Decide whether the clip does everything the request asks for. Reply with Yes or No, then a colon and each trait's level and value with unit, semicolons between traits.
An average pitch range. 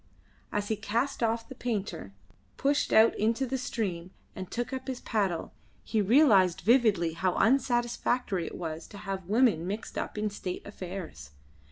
Yes: average, 4.6 semitones